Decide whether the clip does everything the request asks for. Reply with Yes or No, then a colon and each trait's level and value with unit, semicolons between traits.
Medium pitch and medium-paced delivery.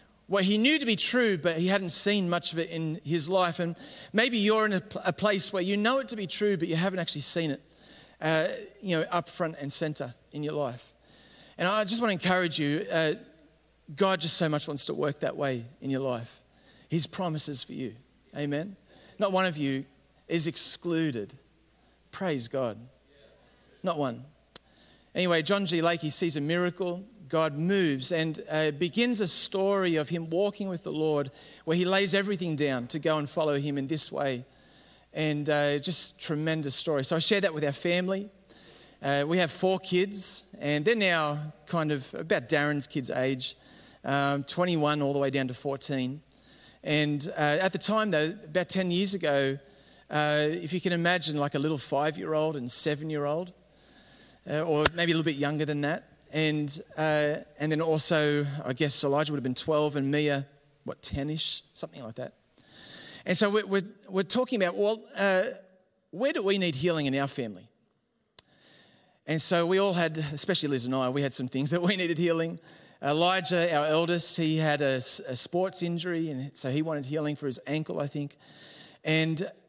Yes: medium, 160 Hz; average, 185 wpm